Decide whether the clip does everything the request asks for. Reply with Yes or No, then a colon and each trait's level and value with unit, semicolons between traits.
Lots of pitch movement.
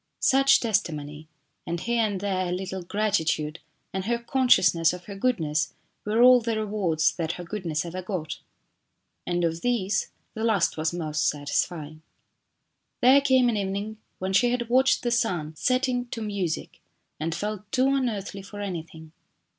Yes: wide, 5.9 semitones